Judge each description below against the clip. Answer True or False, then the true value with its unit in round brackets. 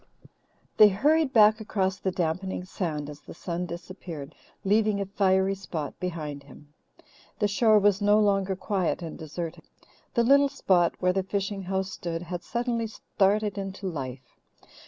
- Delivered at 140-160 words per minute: True (155 wpm)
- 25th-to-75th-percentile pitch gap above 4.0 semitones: False (3.3 semitones)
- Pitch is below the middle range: False (190 Hz)